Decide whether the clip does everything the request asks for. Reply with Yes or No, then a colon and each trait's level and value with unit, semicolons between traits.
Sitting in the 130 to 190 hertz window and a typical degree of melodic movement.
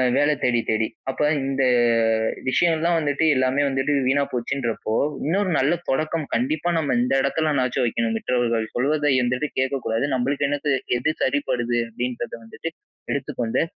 Yes: low, 135 Hz; average, 3.4 semitones